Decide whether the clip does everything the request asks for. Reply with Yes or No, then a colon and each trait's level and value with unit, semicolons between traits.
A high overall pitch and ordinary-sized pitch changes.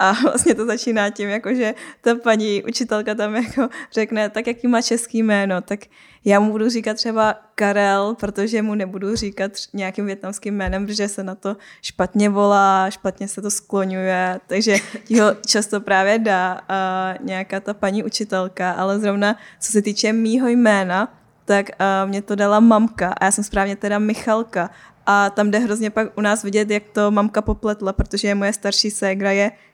No: high, 205 Hz; narrow, 1.7 semitones